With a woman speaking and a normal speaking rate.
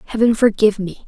Yes: female; average, 170 wpm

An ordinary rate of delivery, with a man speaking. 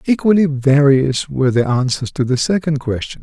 Yes: average, 170 wpm; male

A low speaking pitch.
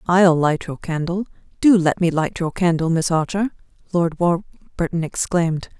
No: medium, 170 Hz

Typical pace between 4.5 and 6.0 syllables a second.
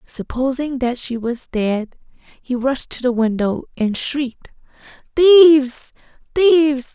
No: 3.8 syllables/s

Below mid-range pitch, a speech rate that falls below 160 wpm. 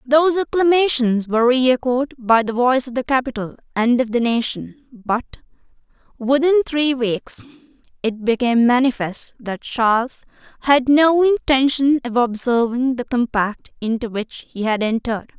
No: very high, 250 Hz; slow, 135 wpm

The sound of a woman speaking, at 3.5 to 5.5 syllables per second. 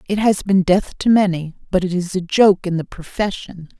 Yes: female; 5.0 syllables/s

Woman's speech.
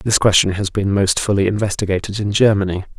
No: male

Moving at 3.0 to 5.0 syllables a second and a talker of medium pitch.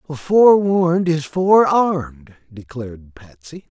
Yes: 4.0 syllables/s; medium, 155 Hz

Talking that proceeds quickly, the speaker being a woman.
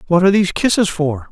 No: fast, 230 wpm; male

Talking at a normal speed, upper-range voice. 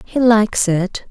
Yes: average, 165 wpm; high, 210 Hz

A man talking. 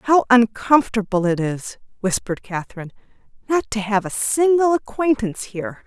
No: female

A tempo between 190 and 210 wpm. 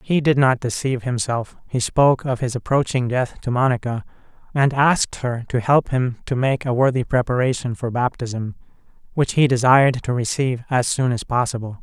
No: average, 180 wpm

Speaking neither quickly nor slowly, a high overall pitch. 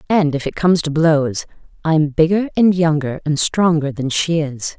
No: average, 190 wpm; medium, 160 Hz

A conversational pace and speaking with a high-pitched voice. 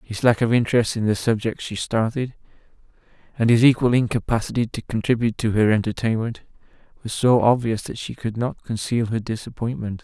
No: average, 165 wpm; low, 115 Hz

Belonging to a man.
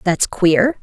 No: female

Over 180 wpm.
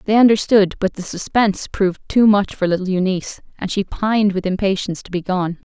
Yes: average, 200 wpm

